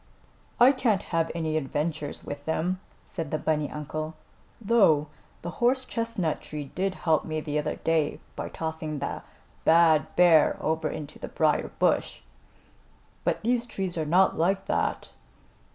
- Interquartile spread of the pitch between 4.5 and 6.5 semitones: No, average, 3.7 semitones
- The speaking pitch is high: No, medium, 160 Hz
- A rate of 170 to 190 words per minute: No, average, 150 wpm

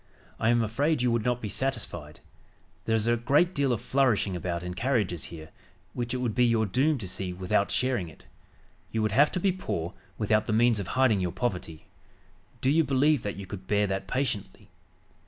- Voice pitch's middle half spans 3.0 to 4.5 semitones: No, average, 5.0 semitones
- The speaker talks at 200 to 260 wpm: Yes, fast, 205 wpm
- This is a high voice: No, low, 115 Hz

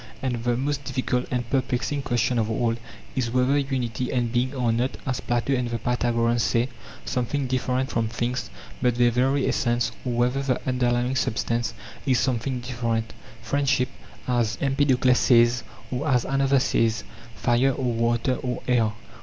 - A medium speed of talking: Yes, average, 160 wpm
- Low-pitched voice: Yes, low, 125 Hz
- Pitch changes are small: Yes, narrow, 1.7 semitones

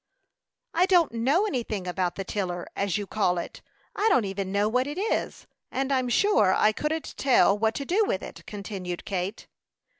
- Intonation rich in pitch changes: Yes, wide, 6.6 semitones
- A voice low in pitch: No, high, 215 Hz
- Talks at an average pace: Yes, average, 185 wpm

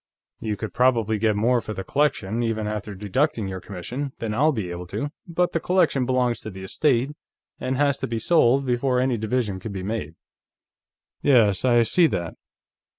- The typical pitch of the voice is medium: No, low, 115 Hz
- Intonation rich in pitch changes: No, average, 4.2 semitones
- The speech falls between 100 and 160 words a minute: No, average, 185 wpm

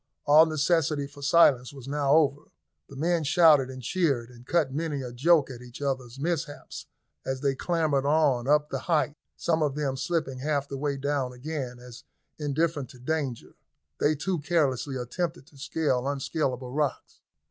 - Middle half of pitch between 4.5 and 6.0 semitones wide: No, average, 3.0 semitones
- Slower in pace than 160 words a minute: No, average, 170 wpm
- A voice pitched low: No, medium, 145 Hz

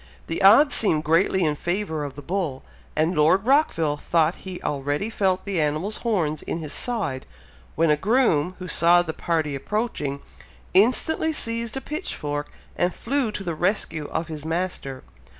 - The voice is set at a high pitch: No, medium, 175 Hz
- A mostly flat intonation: No, wide, 5.6 semitones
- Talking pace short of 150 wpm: No, average, 165 wpm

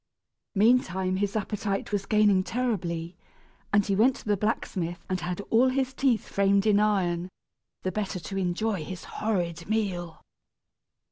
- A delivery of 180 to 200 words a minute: No, average, 145 wpm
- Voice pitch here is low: No, high, 200 Hz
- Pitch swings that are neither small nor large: Yes, average, 3.0 semitones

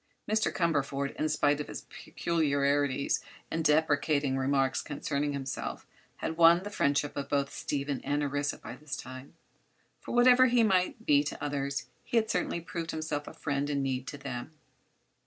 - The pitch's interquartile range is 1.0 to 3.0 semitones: Yes, average, 2.7 semitones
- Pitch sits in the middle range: Yes, medium, 145 Hz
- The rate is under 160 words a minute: No, average, 165 wpm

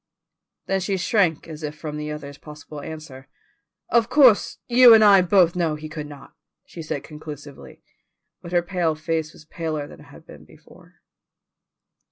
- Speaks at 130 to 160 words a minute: No, average, 170 wpm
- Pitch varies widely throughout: No, average, 3.5 semitones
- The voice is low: No, medium, 160 Hz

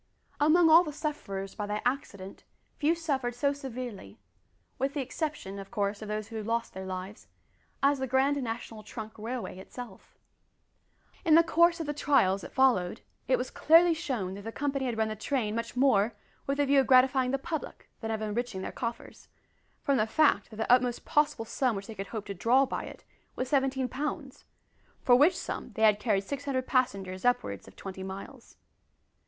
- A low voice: No, high, 245 Hz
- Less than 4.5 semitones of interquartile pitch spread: No, average, 4.9 semitones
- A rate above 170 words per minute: Yes, average, 190 wpm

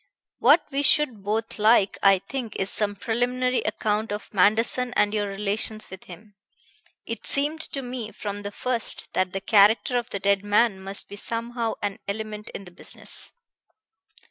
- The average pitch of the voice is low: No, high, 210 Hz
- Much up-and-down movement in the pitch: No, average, 3.0 semitones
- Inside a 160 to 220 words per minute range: Yes, average, 170 wpm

